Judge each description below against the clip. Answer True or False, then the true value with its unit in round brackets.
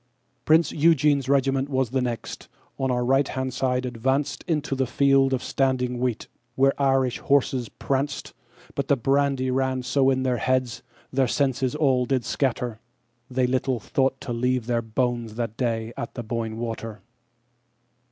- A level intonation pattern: True (2.0 semitones)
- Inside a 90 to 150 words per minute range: True (145 wpm)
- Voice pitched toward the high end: False (130 Hz)